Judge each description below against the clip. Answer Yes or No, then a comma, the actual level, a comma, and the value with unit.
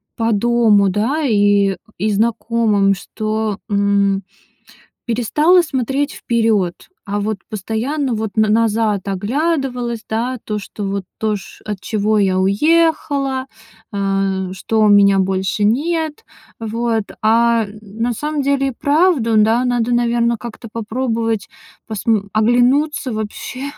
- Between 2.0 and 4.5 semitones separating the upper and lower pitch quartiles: Yes, average, 3.4 semitones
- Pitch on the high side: Yes, high, 225 Hz